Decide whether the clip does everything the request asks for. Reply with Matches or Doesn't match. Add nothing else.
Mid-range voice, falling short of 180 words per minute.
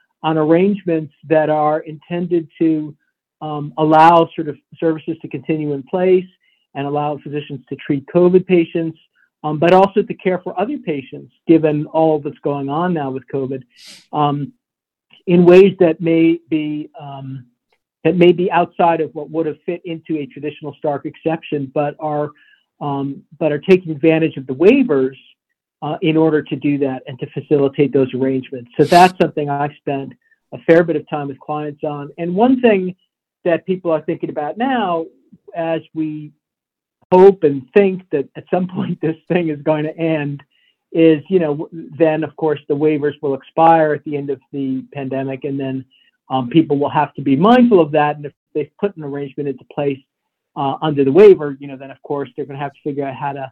Doesn't match